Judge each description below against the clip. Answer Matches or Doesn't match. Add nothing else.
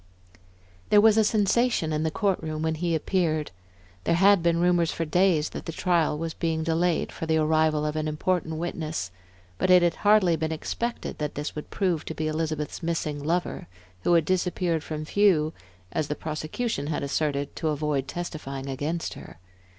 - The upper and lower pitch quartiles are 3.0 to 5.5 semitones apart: Doesn't match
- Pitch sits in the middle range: Matches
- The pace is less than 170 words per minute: Doesn't match